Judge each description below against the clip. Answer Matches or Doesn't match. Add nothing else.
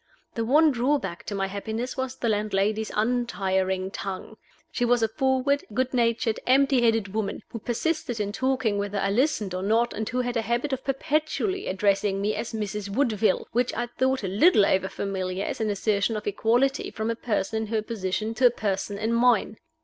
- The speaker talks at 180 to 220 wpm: Matches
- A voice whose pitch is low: Doesn't match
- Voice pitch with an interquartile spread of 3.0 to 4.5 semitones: Matches